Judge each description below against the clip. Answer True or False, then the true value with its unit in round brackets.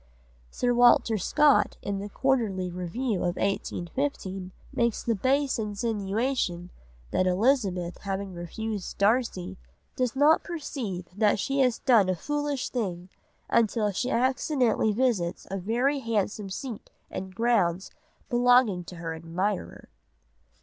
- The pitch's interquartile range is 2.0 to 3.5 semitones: False (5.1 semitones)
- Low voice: False (215 Hz)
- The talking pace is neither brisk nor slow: False (120 wpm)